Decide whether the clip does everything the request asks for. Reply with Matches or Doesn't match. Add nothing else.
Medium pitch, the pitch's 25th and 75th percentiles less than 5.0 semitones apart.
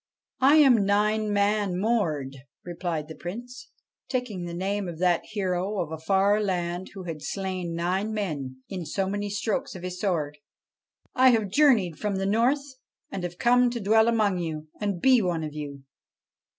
Doesn't match